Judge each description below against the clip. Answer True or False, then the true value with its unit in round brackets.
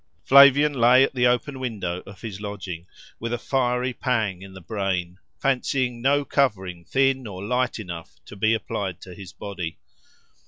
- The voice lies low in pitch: True (115 Hz)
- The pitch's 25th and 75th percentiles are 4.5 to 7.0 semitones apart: True (5.2 semitones)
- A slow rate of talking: False (165 wpm)